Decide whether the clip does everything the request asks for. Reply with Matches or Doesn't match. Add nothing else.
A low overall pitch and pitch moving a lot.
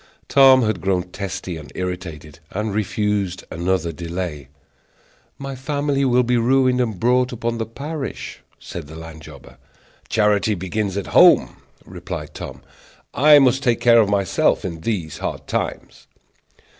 Matches